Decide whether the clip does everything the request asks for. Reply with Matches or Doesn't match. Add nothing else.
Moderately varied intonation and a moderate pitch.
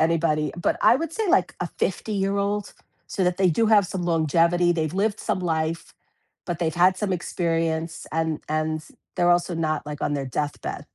Matches